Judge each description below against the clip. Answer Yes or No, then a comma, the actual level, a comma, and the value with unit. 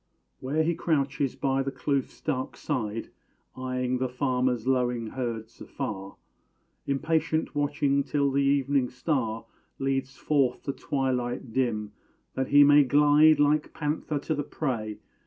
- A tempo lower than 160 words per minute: Yes, slow, 135 wpm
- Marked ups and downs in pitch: No, narrow, 2.5 semitones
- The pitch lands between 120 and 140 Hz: Yes, low, 135 Hz